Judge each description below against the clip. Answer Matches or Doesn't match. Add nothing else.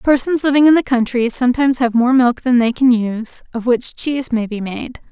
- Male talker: Doesn't match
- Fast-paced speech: Matches